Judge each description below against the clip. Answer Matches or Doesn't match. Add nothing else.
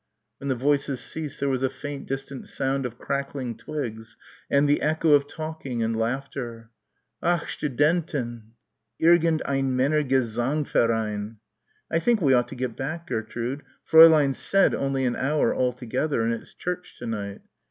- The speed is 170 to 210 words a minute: Doesn't match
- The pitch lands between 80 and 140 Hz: Matches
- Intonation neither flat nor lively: Matches